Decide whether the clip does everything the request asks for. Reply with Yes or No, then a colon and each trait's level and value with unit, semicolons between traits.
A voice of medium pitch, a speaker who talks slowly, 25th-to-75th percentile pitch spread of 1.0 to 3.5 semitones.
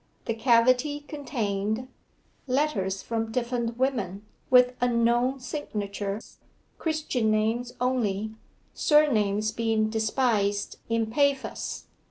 No: high, 230 Hz; slow, 90 wpm; average, 3.0 semitones